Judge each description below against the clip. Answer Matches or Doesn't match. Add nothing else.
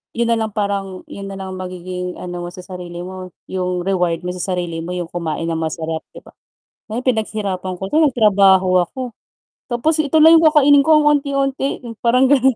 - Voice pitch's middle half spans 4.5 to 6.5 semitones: Matches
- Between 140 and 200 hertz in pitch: Matches